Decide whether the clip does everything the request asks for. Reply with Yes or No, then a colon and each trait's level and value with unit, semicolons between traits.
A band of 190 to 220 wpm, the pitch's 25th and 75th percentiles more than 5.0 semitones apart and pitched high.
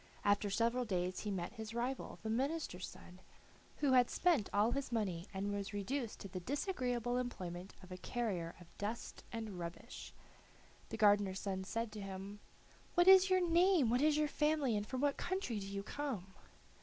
No: average, 180 wpm; wide, 5.6 semitones; high, 220 Hz